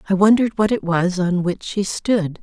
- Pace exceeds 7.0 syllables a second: No, 5.0 syllables/s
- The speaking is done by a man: No, female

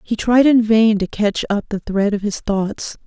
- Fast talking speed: Yes, fast, 235 wpm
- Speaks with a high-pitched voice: Yes, high, 210 Hz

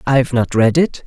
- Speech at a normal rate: No, fast, 225 wpm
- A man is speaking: Yes, male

